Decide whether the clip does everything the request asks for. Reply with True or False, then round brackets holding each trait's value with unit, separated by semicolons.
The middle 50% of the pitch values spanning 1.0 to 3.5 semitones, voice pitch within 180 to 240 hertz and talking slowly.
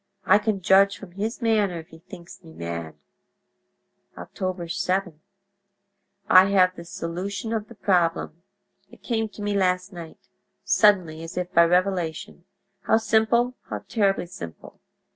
True (3.1 semitones; 190 Hz; 125 wpm)